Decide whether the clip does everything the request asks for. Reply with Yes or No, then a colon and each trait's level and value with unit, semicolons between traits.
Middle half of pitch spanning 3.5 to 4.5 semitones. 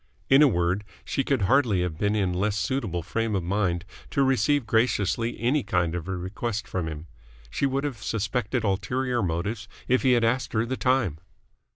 No: wide, 5.5 semitones